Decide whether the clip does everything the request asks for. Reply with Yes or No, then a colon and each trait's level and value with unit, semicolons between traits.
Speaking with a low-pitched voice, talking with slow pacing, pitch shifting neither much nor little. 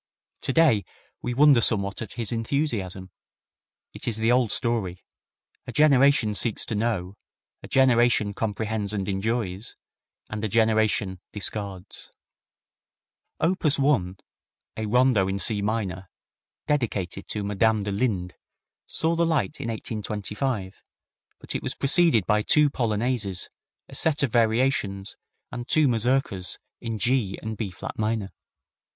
Yes: low, 110 Hz; slow, 130 wpm; average, 4.0 semitones